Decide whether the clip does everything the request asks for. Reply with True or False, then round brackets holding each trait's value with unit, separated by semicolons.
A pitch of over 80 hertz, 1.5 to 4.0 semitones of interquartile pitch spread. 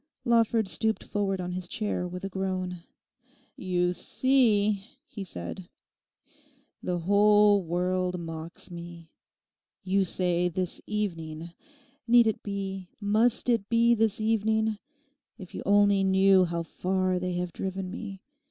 True (190 Hz; 2.8 semitones)